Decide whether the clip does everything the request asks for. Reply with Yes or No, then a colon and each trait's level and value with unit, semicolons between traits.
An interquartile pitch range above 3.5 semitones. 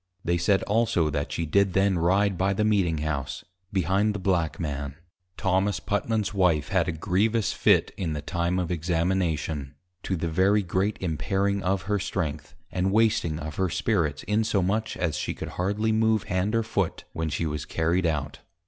Yes: average, 3.9 semitones